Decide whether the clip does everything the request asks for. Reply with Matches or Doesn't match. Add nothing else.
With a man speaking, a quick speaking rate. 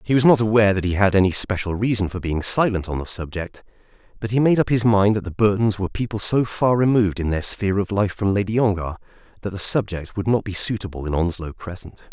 Matches